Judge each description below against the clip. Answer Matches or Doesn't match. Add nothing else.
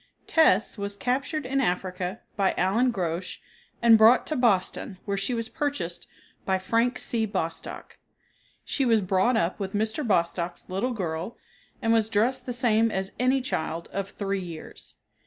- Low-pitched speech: Doesn't match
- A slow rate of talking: Doesn't match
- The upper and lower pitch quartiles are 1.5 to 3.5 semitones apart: Doesn't match